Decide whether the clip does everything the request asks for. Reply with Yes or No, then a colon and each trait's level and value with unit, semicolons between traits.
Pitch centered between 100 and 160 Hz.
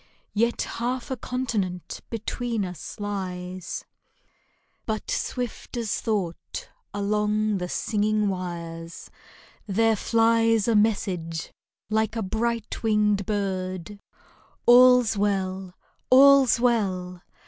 No: high, 210 Hz